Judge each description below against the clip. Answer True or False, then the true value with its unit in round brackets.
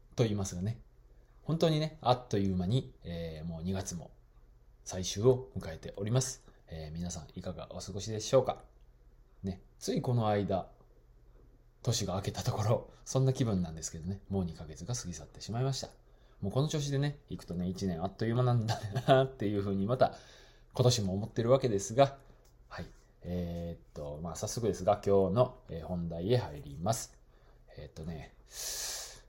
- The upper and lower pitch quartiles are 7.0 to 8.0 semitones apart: False (5.4 semitones)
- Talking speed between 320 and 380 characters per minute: True (340 characters per minute)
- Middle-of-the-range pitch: False (105 Hz)